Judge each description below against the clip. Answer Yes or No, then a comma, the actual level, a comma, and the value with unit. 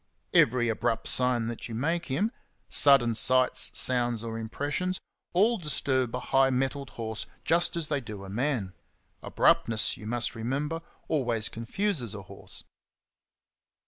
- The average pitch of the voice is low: Yes, low, 125 Hz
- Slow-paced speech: No, average, 150 wpm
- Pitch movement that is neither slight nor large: Yes, average, 4.2 semitones